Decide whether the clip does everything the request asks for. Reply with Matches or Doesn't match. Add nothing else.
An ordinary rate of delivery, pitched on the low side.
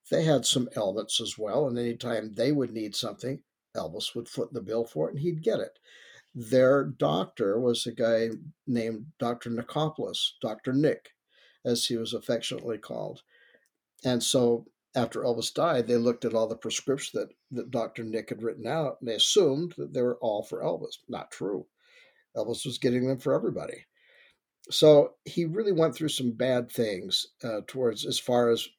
Matches